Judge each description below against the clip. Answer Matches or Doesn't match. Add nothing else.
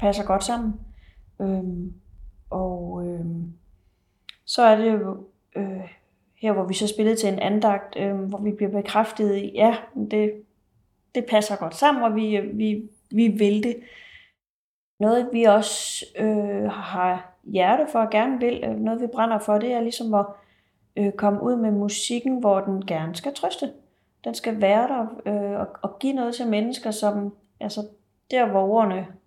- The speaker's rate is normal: Matches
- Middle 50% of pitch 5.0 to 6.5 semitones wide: Doesn't match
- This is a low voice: Doesn't match